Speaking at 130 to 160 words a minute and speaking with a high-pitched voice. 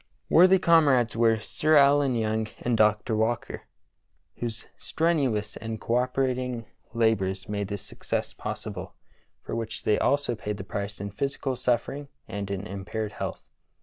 No: average, 150 wpm; low, 115 Hz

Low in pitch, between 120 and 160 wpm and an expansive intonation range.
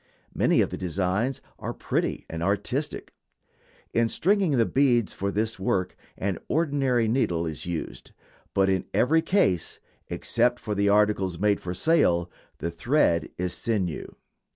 Yes: low, 105 Hz; average, 140 wpm; wide, 5.7 semitones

